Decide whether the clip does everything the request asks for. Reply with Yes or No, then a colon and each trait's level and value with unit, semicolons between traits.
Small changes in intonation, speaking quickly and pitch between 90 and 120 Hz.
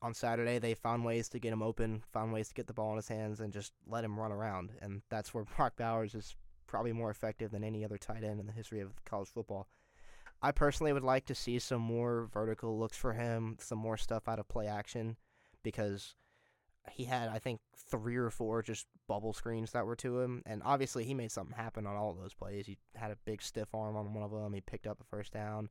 Yes: narrow, 1.7 semitones; fast, 245 wpm; low, 110 Hz